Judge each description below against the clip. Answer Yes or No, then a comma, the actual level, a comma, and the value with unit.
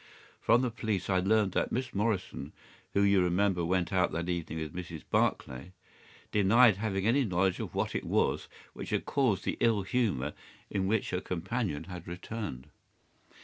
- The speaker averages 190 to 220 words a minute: No, average, 170 wpm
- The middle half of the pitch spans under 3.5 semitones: No, average, 3.9 semitones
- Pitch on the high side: No, very low, 95 Hz